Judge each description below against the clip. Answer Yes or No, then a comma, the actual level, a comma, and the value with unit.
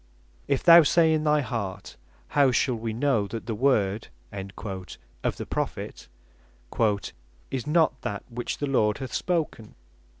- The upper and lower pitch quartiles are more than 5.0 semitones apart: Yes, wide, 5.5 semitones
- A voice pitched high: No, low, 125 Hz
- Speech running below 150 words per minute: Yes, average, 140 wpm